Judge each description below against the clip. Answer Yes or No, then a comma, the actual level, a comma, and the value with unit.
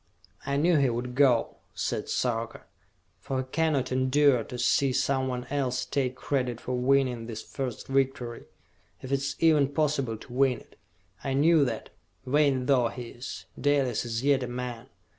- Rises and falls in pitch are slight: Yes, narrow, 2.1 semitones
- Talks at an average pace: Yes, average, 165 wpm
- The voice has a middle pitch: No, low, 130 Hz